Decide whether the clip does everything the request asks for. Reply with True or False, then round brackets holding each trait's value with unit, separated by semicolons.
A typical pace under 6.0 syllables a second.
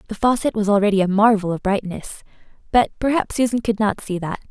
False (6.1 syllables/s)